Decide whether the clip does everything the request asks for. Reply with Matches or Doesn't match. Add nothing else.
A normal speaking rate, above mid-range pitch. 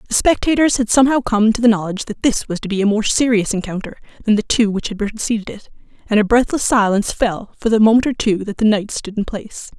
Doesn't match